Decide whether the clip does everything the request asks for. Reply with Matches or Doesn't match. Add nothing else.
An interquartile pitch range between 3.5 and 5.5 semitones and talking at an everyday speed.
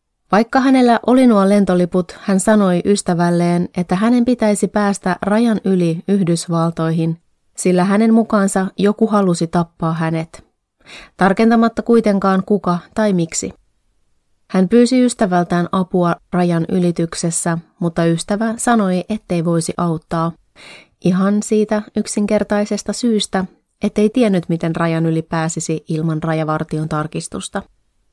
Matches